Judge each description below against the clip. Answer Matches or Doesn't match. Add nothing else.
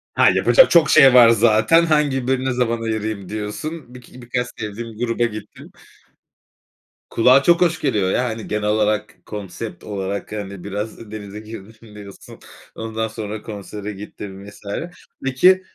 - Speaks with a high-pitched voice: Doesn't match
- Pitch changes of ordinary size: Matches